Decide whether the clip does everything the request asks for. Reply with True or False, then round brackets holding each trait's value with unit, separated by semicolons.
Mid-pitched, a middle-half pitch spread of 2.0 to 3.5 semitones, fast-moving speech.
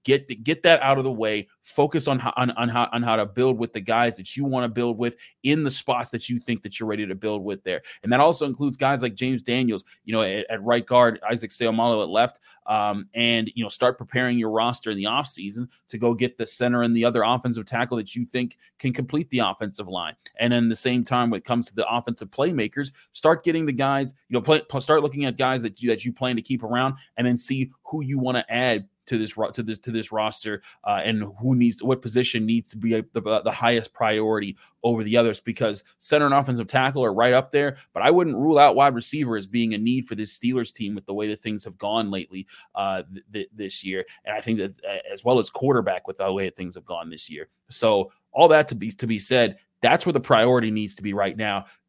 False (120 Hz; 2.8 semitones; 255 wpm)